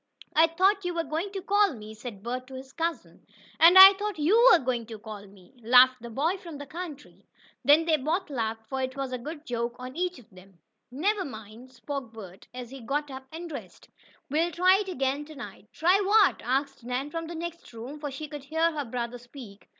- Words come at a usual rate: No, fast, 220 wpm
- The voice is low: No, very high, 275 Hz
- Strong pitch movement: Yes, wide, 5.7 semitones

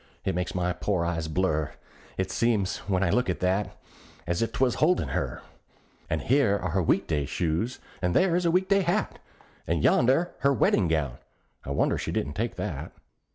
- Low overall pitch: Yes, very low, 95 Hz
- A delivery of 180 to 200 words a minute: Yes, average, 195 wpm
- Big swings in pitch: Yes, wide, 6.9 semitones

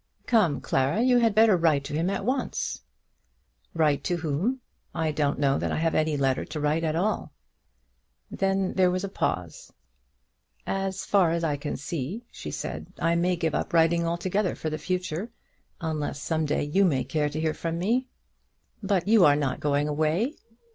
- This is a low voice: No, medium, 165 Hz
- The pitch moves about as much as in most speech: Yes, average, 4.5 semitones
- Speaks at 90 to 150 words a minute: No, average, 180 wpm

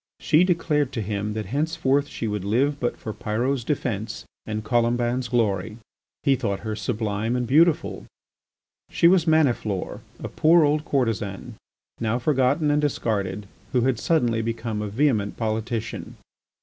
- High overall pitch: No, low, 120 Hz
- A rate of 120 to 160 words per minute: Yes, average, 145 wpm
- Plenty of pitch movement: No, average, 5.0 semitones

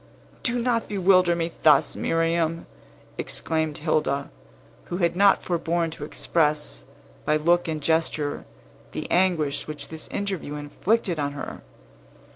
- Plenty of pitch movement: No, average, 2.7 semitones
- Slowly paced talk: Yes, slow, 125 wpm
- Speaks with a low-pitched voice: No, medium, 165 Hz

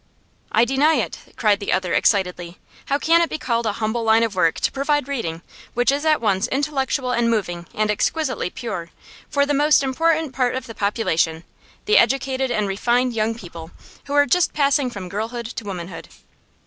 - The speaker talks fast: No, average, 185 wpm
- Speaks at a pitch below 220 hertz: No, high, 235 Hz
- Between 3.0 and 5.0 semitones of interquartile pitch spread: No, wide, 5.6 semitones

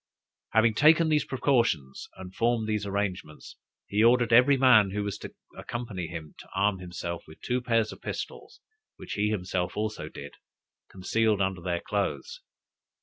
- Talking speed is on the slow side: No, average, 155 wpm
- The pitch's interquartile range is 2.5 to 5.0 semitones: Yes, average, 4.2 semitones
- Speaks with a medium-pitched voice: No, low, 105 Hz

